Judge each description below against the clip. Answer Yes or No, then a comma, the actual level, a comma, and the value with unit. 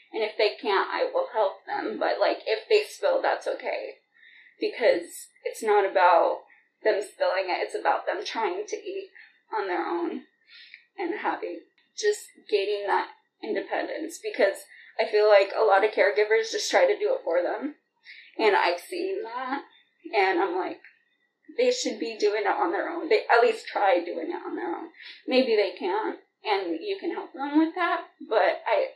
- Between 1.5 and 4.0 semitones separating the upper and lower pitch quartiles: No, average, 4.5 semitones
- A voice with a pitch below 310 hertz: No, very high, 395 Hz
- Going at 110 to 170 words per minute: No, average, 180 wpm